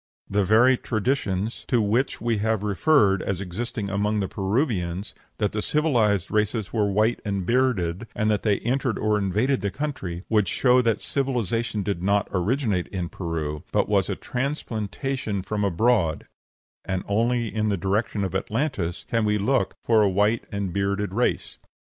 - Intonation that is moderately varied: Yes, average, 3.4 semitones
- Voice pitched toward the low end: Yes, low, 105 Hz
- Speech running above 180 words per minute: No, average, 165 wpm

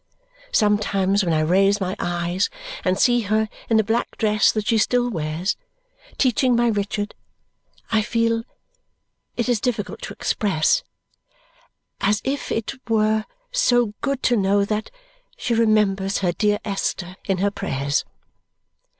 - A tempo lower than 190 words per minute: Yes, average, 140 wpm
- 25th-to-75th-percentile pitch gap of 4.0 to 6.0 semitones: No, average, 2.9 semitones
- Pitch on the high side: Yes, high, 210 Hz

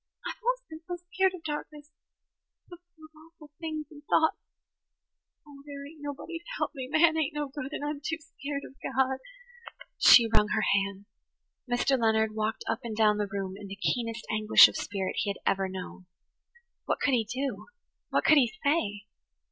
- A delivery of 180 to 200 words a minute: Yes, average, 190 wpm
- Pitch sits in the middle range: No, very high, 275 Hz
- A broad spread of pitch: Yes, wide, 6.4 semitones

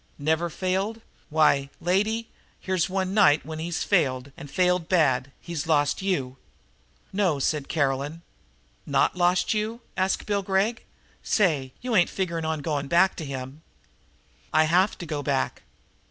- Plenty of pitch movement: No, average, 4.6 semitones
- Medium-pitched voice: Yes, medium, 170 Hz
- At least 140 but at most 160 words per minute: Yes, average, 145 wpm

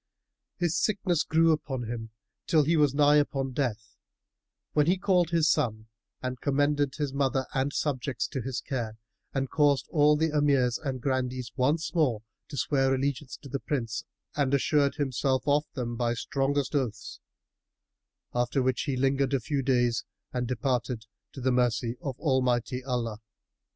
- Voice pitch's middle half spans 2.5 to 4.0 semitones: Yes, average, 2.9 semitones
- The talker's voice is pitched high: No, low, 135 Hz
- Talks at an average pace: Yes, average, 155 wpm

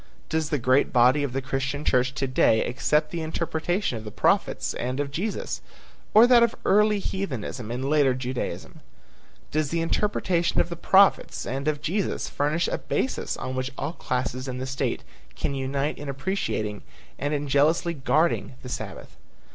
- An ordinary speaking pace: Yes, average, 170 wpm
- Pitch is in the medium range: Yes, medium, 145 Hz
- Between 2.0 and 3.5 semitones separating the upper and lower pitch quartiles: No, average, 4.5 semitones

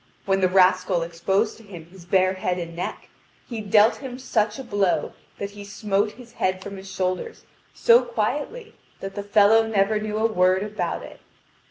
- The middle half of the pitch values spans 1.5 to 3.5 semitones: Yes, average, 2.8 semitones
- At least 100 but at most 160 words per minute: No, average, 185 wpm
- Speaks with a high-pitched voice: Yes, high, 200 Hz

